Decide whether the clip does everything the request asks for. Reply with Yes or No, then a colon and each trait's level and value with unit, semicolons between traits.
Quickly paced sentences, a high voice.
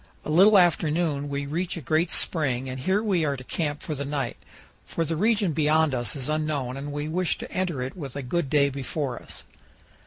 No: fast, 220 wpm; medium, 150 Hz